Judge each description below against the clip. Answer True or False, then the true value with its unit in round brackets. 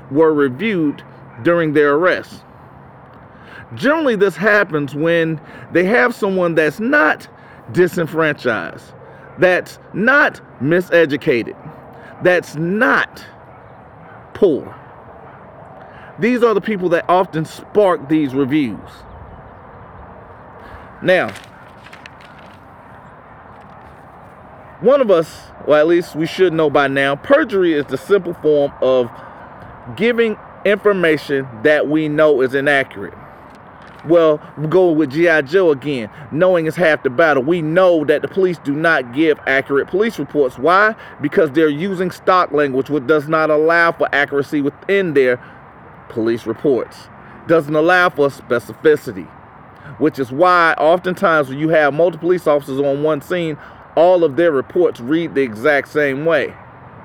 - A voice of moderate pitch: True (155 Hz)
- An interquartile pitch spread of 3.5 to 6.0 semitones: True (3.9 semitones)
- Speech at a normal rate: False (125 wpm)